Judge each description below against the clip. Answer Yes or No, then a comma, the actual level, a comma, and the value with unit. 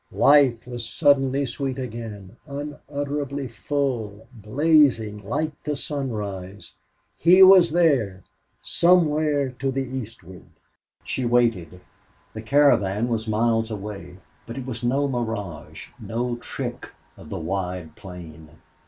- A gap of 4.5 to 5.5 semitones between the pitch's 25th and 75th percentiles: Yes, average, 5.2 semitones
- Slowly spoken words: Yes, slow, 115 wpm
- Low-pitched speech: Yes, low, 120 Hz